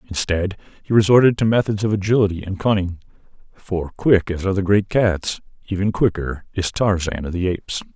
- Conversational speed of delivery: Yes, average, 175 wpm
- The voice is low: Yes, very low, 95 Hz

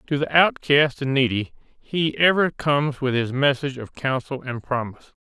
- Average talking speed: Yes, average, 170 wpm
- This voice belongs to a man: Yes, male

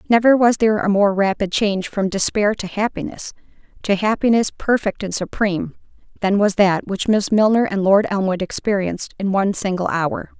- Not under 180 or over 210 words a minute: No, average, 160 wpm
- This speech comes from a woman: Yes, female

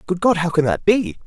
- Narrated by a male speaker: Yes, male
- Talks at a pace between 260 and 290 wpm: Yes, fast, 285 wpm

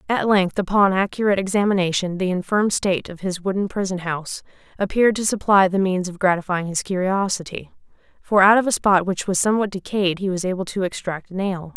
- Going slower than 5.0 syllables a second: No, 6.0 syllables/s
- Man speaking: No, female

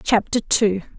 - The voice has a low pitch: No, high, 210 Hz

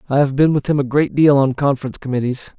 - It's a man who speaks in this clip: Yes, male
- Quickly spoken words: Yes, fast, 255 wpm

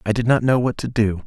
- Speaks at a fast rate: Yes, fast, 330 wpm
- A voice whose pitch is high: No, low, 115 Hz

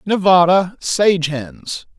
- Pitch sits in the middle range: Yes, medium, 180 Hz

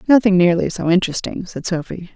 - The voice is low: No, medium, 185 Hz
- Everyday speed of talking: Yes, average, 165 wpm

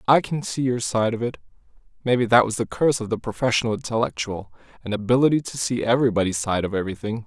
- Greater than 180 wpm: Yes, average, 200 wpm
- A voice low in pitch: Yes, low, 115 Hz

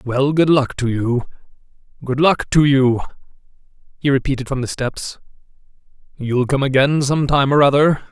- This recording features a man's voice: Yes, male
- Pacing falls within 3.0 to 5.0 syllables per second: Yes, 4.8 syllables/s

